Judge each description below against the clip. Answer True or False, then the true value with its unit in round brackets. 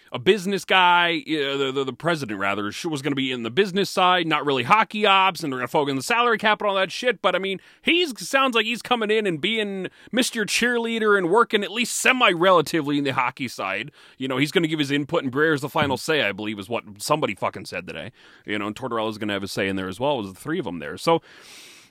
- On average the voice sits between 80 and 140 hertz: False (165 Hz)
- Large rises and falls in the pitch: True (7.6 semitones)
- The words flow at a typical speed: False (270 wpm)